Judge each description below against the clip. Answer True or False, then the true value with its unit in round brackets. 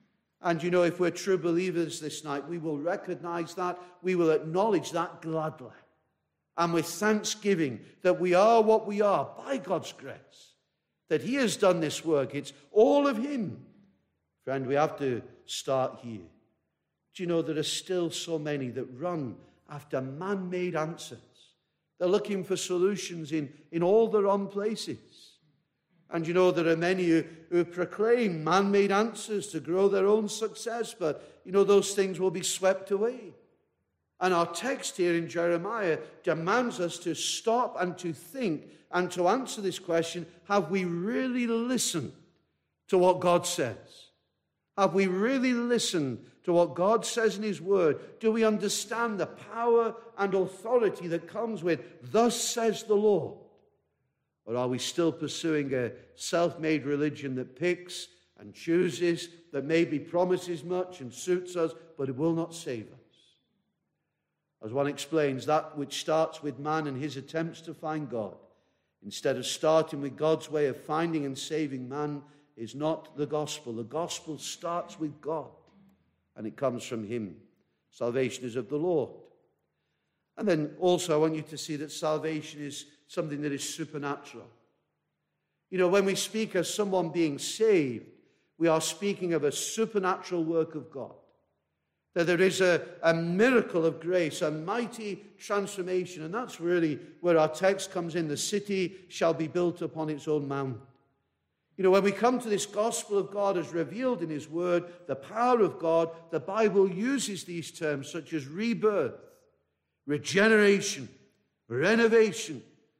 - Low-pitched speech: False (170 Hz)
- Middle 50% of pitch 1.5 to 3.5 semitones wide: False (4.6 semitones)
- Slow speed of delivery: False (165 wpm)